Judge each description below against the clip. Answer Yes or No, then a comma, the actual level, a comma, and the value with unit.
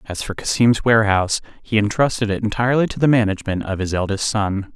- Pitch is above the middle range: No, low, 105 Hz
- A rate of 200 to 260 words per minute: No, average, 190 wpm